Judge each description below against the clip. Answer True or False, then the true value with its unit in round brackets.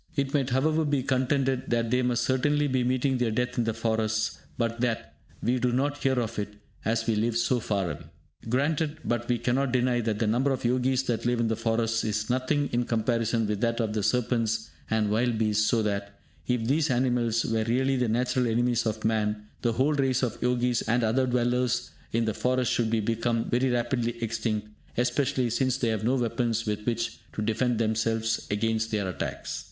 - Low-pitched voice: True (120 Hz)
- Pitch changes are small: True (2.2 semitones)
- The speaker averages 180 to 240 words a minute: True (200 wpm)